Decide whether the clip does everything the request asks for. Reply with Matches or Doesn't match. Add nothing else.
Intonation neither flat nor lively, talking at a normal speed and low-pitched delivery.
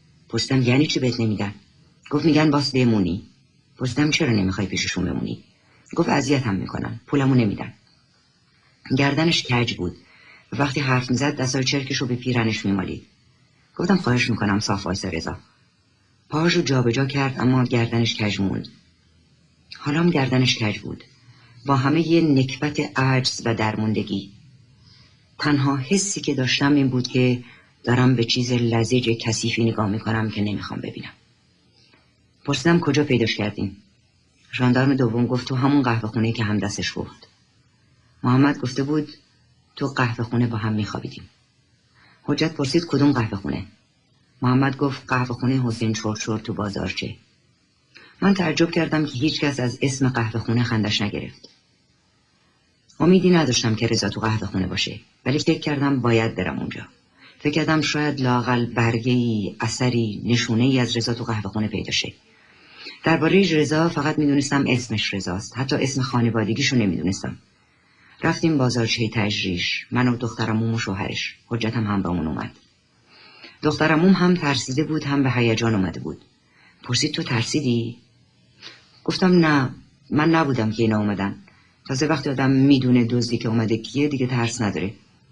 Matches